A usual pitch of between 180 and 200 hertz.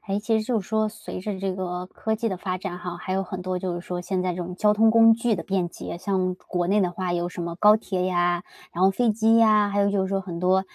Yes: high, 190 Hz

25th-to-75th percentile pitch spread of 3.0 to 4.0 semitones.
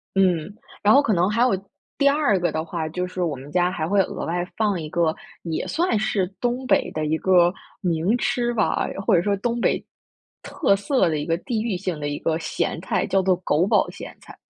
No: average, 4.9 semitones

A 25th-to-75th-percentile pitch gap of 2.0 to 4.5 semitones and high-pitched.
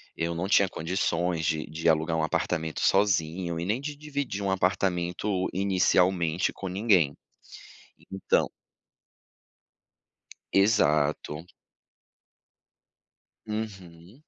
No: average, 3.2 semitones; very low, 90 Hz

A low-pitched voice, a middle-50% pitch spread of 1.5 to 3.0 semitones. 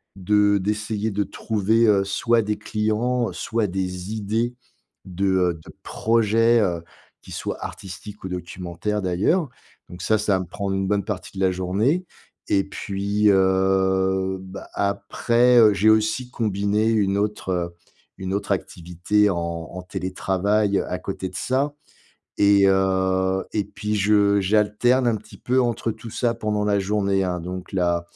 Yes: low, 100 Hz; narrow, 2.4 semitones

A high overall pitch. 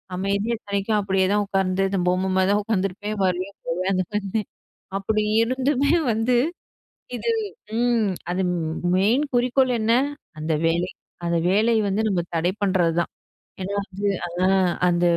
Yes: high, 195 Hz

